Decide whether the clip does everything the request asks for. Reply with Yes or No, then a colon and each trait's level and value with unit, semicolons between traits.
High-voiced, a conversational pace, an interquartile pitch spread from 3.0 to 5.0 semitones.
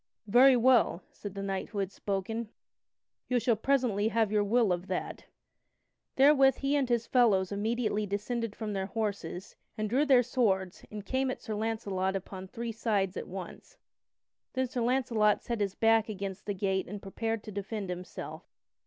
Yes: high, 215 Hz; average, 170 wpm; average, 3.5 semitones